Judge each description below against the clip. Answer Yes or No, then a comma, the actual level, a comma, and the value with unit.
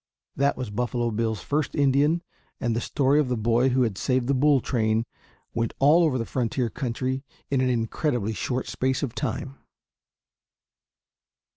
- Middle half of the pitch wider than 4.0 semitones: No, average, 3.0 semitones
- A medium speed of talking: Yes, average, 160 wpm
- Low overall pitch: Yes, low, 130 Hz